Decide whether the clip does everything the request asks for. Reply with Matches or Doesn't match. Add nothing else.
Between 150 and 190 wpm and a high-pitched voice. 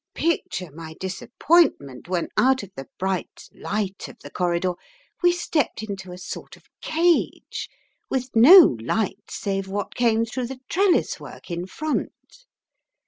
Doesn't match